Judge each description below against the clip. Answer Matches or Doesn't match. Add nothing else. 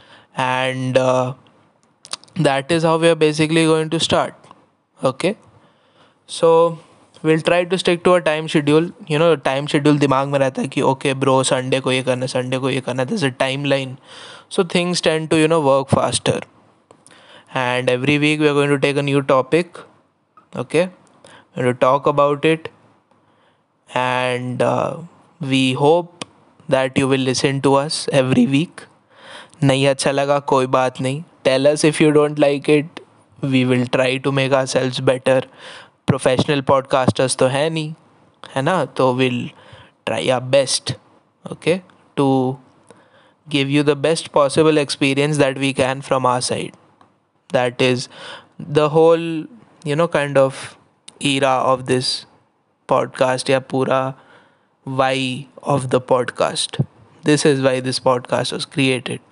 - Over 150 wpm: Doesn't match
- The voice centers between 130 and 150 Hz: Matches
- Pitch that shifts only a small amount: Doesn't match